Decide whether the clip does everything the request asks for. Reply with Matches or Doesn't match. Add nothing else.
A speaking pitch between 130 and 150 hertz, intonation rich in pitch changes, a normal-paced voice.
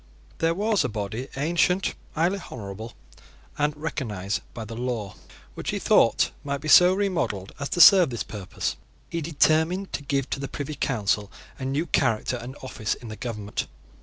Matches